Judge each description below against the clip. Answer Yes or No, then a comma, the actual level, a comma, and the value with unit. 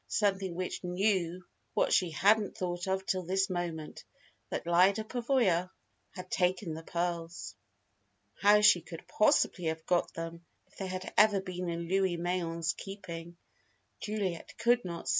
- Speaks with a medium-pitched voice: Yes, medium, 180 Hz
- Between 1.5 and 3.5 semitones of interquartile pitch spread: Yes, narrow, 2.4 semitones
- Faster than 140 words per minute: Yes, average, 150 wpm